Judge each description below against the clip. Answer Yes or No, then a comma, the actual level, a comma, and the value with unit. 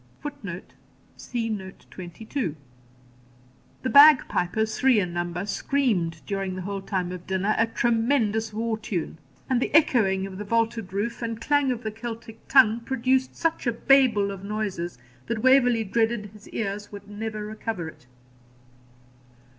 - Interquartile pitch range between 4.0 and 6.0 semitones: No, average, 3.4 semitones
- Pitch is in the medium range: No, high, 220 Hz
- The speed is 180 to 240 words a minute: No, average, 150 wpm